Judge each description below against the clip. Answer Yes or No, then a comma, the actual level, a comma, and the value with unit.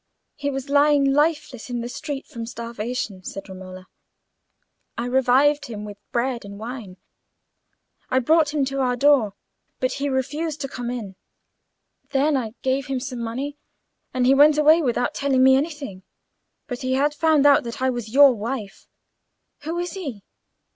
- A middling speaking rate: Yes, average, 165 wpm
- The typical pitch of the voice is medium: No, very high, 260 Hz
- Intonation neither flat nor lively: Yes, average, 3.5 semitones